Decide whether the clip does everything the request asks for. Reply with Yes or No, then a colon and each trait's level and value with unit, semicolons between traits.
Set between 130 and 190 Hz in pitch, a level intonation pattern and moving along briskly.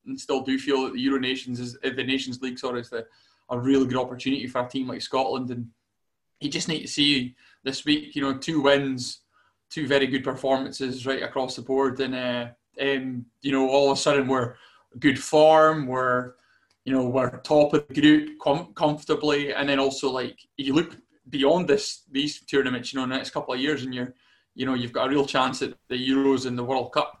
Yes: low, 135 Hz; narrow, 2.0 semitones; fast, 215 wpm